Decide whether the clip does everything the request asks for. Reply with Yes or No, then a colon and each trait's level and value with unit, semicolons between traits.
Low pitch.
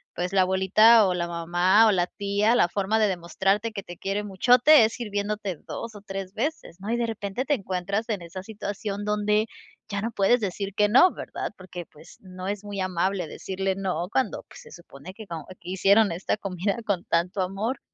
No: high, 195 Hz